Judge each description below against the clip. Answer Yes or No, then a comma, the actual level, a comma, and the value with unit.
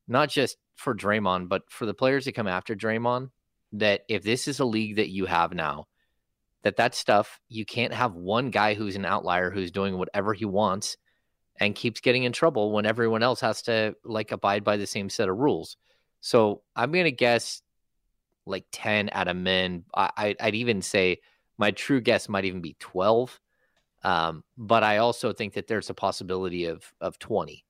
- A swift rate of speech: No, average, 195 wpm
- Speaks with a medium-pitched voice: No, low, 105 Hz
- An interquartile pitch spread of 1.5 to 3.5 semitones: Yes, average, 3.1 semitones